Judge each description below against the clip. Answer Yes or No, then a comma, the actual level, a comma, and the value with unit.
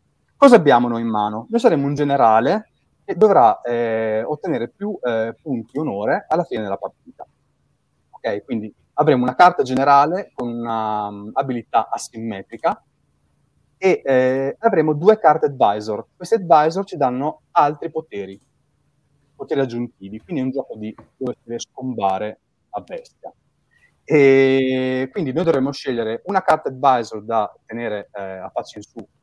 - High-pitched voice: No, low, 130 Hz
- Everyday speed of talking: Yes, average, 145 wpm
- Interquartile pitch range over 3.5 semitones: Yes, wide, 5.4 semitones